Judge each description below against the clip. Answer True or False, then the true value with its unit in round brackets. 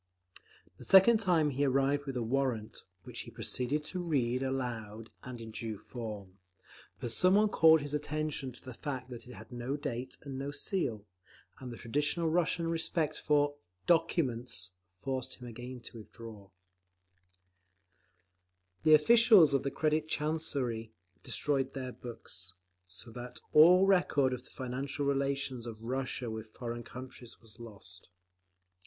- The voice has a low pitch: True (130 Hz)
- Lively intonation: False (4.2 semitones)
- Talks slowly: False (145 wpm)